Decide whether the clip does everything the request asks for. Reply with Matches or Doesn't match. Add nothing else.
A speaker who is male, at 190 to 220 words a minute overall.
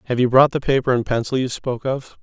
Doesn't match